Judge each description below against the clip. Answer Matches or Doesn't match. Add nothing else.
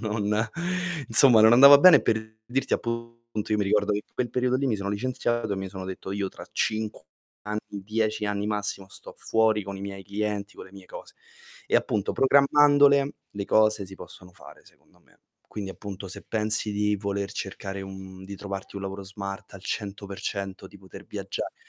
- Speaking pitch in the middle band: Doesn't match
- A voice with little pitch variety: Matches